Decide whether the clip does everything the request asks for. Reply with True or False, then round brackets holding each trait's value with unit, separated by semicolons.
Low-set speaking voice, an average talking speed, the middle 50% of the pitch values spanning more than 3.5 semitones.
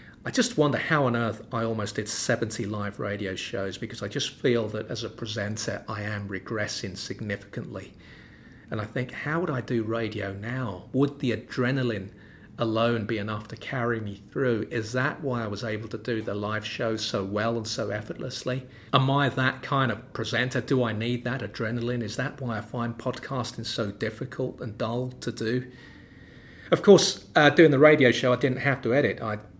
False (115 Hz; 195 wpm; 3.0 semitones)